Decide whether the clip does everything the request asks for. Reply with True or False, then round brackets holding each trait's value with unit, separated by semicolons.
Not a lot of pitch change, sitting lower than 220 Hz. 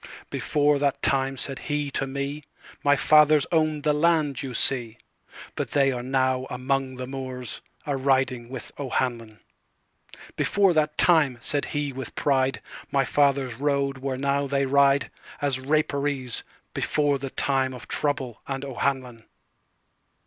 True (1.8 semitones; 135 Hz)